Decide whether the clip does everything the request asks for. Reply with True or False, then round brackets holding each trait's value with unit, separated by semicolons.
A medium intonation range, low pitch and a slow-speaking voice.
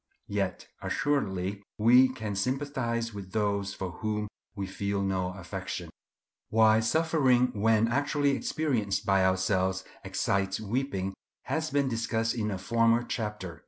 True (4.0 semitones; 110 Hz; 125 wpm)